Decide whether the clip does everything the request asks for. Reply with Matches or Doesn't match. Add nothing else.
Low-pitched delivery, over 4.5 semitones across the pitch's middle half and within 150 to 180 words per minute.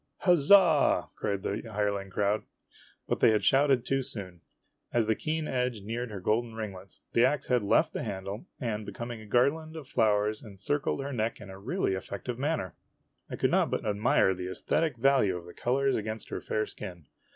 Doesn't match